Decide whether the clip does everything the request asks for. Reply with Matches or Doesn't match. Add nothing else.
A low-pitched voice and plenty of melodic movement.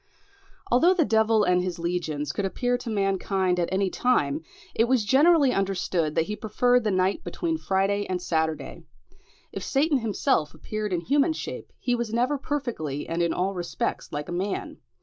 Doesn't match